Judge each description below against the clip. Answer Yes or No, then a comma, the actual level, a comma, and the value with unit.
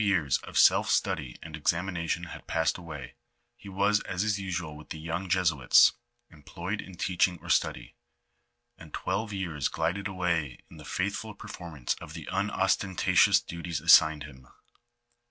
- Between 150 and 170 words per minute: Yes, average, 155 wpm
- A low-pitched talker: Yes, very low, 85 Hz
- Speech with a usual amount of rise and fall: Yes, average, 3.6 semitones